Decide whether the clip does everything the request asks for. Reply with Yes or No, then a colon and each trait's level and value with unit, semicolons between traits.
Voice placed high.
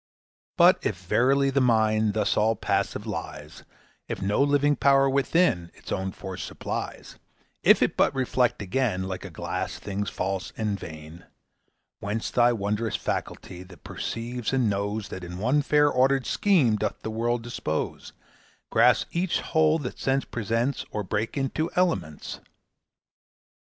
No: low, 115 Hz